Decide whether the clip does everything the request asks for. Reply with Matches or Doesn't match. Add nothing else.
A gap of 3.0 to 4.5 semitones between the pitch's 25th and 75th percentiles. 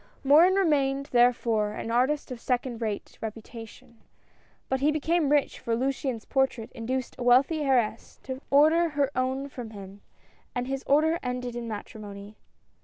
Matches